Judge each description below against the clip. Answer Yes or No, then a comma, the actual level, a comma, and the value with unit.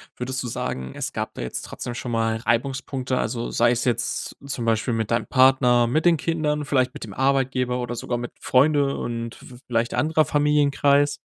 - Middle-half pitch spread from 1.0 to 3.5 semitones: Yes, average, 2.9 semitones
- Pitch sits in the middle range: No, low, 125 Hz